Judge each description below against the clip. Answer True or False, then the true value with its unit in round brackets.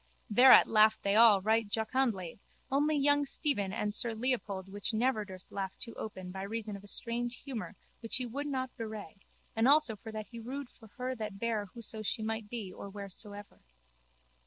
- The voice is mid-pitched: False (220 Hz)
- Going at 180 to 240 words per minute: True (185 wpm)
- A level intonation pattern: False (3.2 semitones)